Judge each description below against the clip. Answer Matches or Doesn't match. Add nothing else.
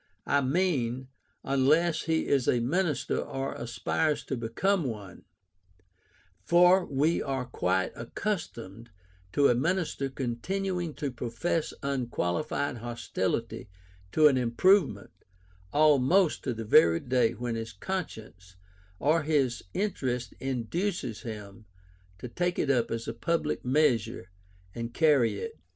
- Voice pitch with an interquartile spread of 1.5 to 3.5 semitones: Doesn't match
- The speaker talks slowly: Matches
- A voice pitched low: Matches